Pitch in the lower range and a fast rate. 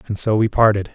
Yes: low, 105 Hz; fast, 255 wpm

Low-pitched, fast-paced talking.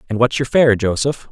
Yes: low, 120 Hz; fast, 230 wpm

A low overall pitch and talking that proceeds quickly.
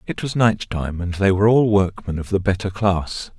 Yes: very low, 95 Hz; fast, 215 wpm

